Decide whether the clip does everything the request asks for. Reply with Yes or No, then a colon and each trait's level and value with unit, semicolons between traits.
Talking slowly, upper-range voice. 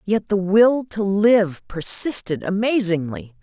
Yes: slow, 125 wpm; high, 200 Hz